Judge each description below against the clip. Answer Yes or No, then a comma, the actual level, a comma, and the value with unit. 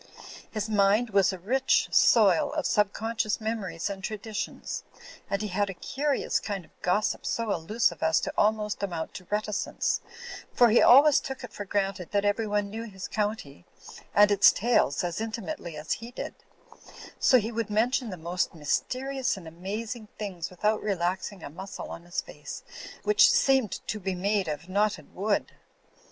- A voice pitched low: No, high, 205 Hz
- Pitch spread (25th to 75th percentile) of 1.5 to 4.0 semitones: Yes, average, 3.3 semitones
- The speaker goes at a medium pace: Yes, average, 170 wpm